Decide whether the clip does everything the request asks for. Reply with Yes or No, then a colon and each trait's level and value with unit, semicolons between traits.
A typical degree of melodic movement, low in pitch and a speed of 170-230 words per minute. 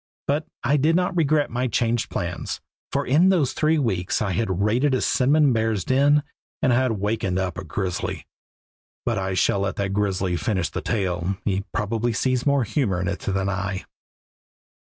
No: wide, 5.9 semitones; low, 110 Hz; average, 175 wpm